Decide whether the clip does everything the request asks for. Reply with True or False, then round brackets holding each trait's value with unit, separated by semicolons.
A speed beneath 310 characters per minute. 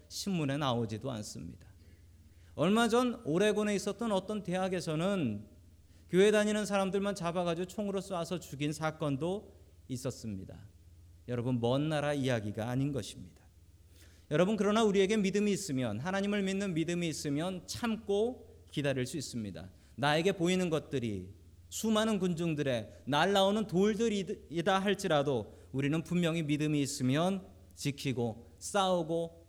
False (320 characters per minute)